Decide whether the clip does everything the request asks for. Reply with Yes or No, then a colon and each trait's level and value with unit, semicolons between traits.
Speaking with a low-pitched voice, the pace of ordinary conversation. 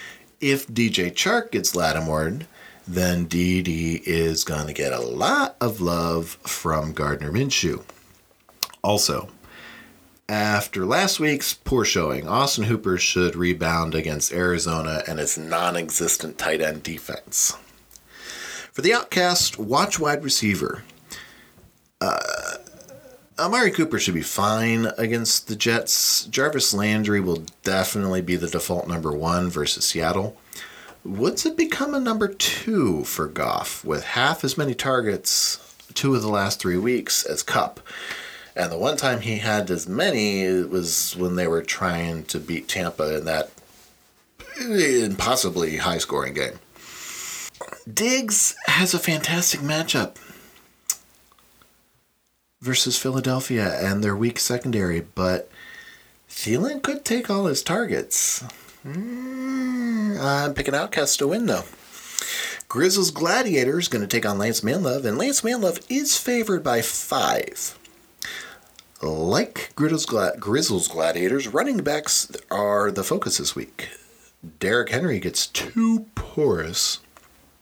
No: low, 105 Hz; slow, 125 wpm